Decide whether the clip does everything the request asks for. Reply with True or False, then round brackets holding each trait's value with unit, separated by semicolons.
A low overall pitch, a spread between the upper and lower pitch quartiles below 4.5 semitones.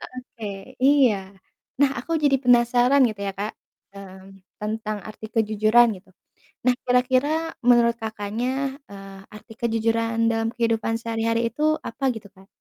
False (225 Hz; 2.4 semitones)